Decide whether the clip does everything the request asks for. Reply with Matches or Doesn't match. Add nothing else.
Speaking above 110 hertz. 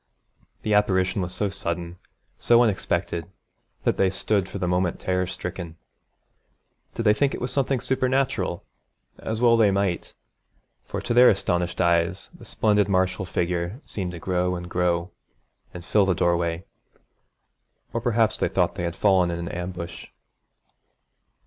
Doesn't match